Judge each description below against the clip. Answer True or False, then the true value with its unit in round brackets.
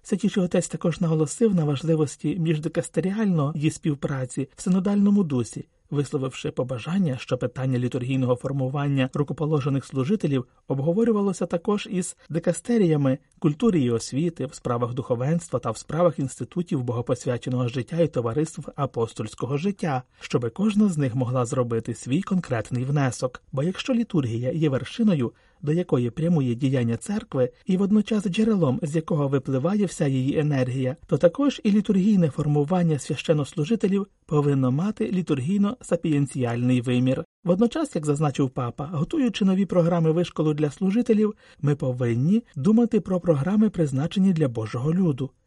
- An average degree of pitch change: False (5.9 semitones)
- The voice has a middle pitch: True (155 Hz)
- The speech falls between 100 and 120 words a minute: False (130 wpm)